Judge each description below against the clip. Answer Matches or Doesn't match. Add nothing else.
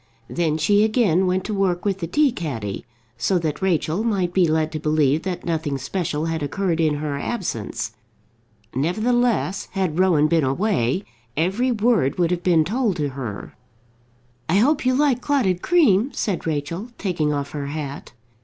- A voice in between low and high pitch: Matches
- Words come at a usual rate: Matches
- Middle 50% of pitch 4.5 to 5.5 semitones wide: Matches